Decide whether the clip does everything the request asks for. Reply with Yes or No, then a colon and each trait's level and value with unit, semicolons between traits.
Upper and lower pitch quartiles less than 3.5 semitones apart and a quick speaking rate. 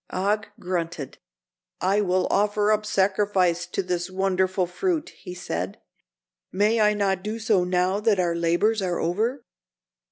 No: average, 2.7 semitones; average, 140 wpm